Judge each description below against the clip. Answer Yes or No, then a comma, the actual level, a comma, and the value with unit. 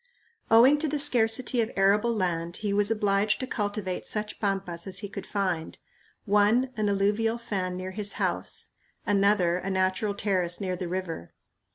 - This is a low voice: No, high, 200 Hz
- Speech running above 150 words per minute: Yes, average, 165 wpm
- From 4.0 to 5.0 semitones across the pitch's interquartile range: No, narrow, 2.6 semitones